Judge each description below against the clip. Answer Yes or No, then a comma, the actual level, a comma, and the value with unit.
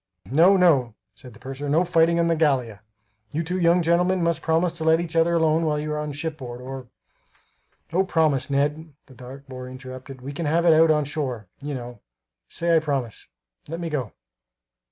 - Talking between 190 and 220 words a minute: Yes, average, 195 wpm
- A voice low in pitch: No, medium, 150 Hz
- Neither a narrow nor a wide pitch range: Yes, average, 3.9 semitones